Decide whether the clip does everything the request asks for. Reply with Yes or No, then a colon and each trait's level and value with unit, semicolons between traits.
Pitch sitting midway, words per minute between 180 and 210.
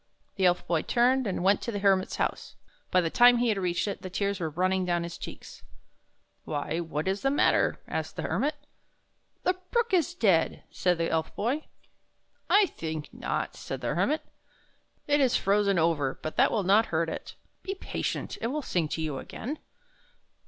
No: high, 195 Hz; average, 200 wpm